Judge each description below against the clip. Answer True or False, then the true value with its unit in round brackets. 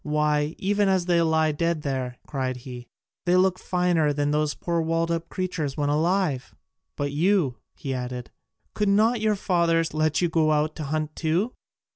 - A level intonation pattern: False (3.4 semitones)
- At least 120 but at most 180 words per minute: True (175 wpm)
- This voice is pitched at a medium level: True (160 Hz)